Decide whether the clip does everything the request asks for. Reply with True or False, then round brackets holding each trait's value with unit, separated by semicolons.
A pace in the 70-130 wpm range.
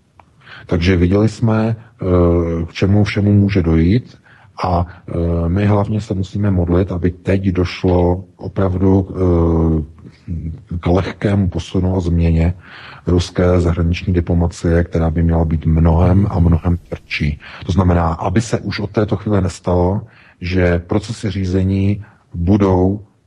True (120 wpm)